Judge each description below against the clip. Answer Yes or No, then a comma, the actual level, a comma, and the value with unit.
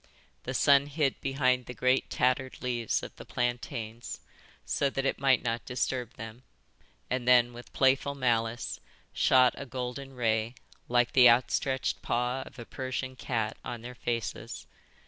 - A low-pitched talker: Yes, low, 125 Hz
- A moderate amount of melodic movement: No, narrow, 1.7 semitones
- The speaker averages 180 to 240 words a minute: No, average, 150 wpm